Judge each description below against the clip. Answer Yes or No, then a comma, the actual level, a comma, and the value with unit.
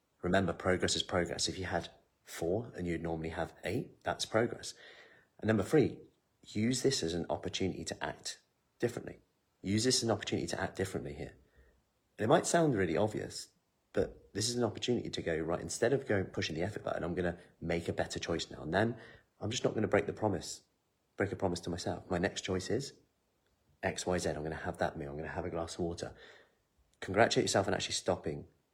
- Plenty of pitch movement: No, average, 3.5 semitones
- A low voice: Yes, very low, 90 Hz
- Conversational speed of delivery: No, fast, 210 wpm